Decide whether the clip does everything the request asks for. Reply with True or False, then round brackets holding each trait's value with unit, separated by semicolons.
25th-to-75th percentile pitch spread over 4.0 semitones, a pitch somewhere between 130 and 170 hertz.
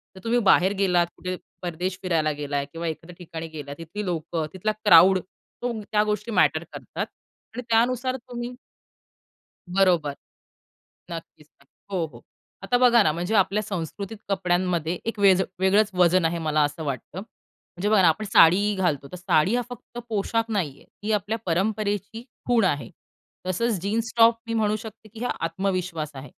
False (4.5 semitones; 190 Hz)